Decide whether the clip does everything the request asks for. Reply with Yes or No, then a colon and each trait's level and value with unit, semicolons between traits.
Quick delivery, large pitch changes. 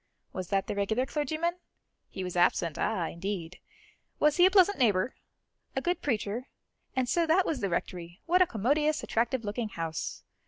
No: average, 170 wpm; wide, 8.6 semitones